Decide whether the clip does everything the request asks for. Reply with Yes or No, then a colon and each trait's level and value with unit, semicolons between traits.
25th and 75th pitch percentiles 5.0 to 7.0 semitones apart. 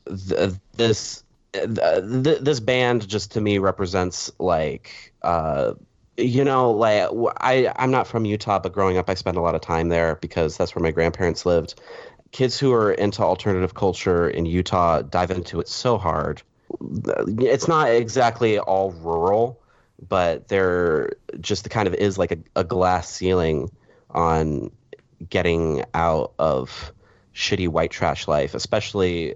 Yes: wide, 5.4 semitones